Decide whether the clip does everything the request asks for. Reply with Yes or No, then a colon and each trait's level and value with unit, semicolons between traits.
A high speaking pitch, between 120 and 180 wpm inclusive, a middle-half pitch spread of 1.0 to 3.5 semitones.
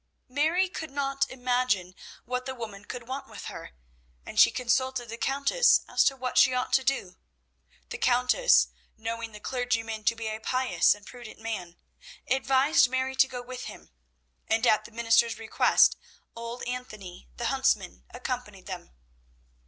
Yes: high, 245 Hz; average, 160 wpm; average, 2.7 semitones